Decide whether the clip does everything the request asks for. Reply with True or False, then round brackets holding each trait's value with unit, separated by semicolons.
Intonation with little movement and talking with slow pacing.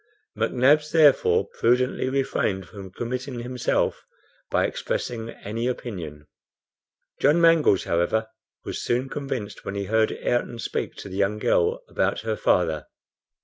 False (4.6 semitones; 130 wpm)